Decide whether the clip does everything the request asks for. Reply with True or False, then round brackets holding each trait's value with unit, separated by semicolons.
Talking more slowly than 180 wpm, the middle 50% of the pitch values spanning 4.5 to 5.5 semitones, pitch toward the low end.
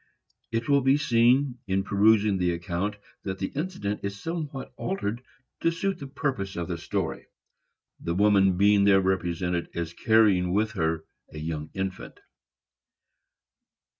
True (140 wpm; 5.0 semitones; 100 Hz)